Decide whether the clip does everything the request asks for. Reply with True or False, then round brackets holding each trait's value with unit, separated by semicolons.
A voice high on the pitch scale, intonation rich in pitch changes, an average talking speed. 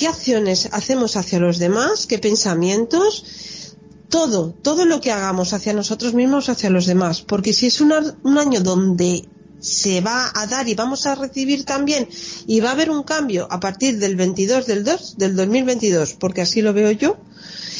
True (220 Hz; 6.2 semitones; 180 wpm)